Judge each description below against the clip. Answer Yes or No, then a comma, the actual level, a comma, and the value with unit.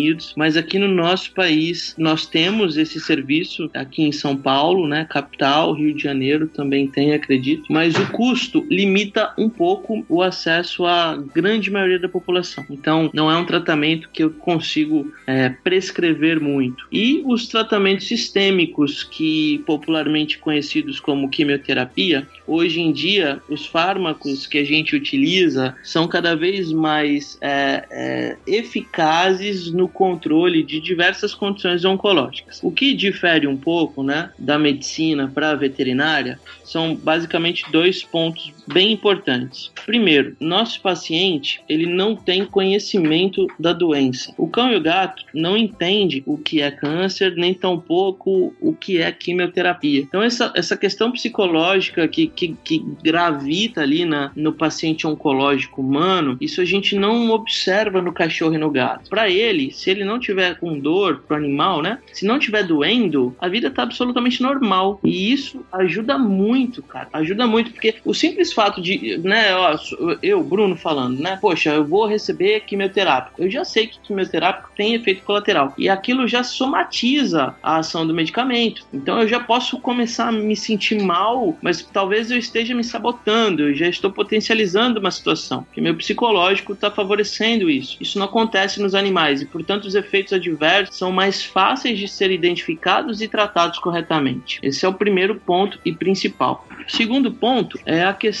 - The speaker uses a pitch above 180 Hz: Yes, high, 190 Hz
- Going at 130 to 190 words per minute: Yes, average, 160 wpm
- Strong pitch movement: Yes, wide, 5.9 semitones